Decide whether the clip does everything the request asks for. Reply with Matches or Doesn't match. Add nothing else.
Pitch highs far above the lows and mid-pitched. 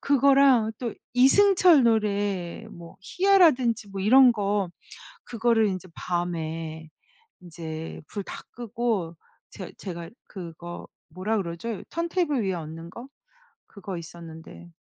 Doesn't match